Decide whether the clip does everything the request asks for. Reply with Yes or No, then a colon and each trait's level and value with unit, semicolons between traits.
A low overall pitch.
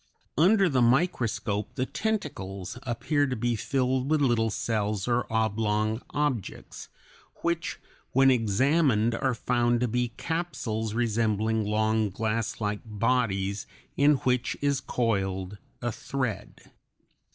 Yes: low, 120 Hz